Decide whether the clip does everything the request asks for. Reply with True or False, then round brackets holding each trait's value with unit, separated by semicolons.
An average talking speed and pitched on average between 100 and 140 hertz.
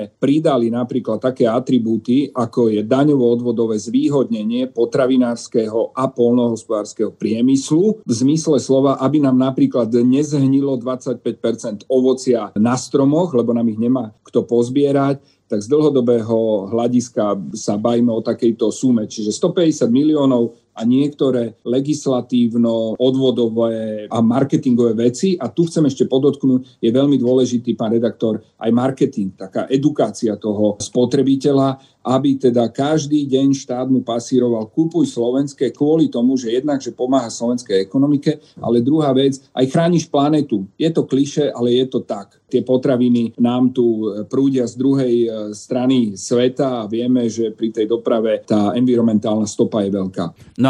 True (135 wpm; 125 Hz)